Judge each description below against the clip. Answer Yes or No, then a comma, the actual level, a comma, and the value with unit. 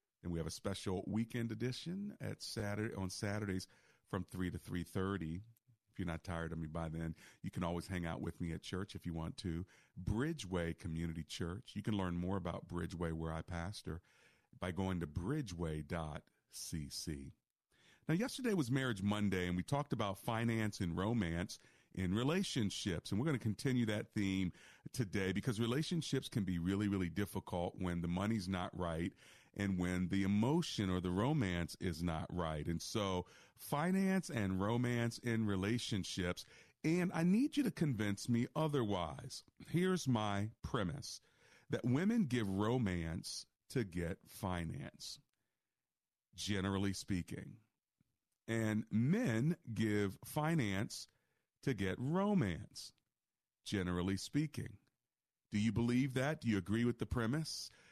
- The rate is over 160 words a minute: No, average, 145 wpm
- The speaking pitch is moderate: No, low, 100 Hz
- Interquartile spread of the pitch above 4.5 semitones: Yes, wide, 5.4 semitones